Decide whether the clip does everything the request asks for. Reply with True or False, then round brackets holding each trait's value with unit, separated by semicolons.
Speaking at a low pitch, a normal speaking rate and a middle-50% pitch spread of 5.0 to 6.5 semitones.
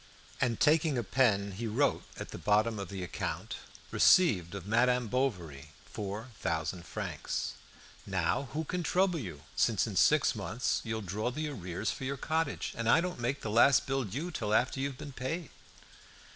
True (120 Hz; 175 wpm; 5.6 semitones)